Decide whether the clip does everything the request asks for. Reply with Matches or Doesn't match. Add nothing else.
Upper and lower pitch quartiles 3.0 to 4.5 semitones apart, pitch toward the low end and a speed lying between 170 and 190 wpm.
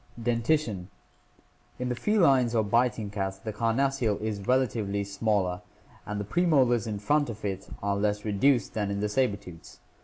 Matches